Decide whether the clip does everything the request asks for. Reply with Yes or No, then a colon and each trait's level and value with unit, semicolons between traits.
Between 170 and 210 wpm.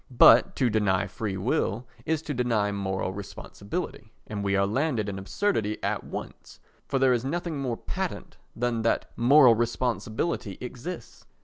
No: average, 145 wpm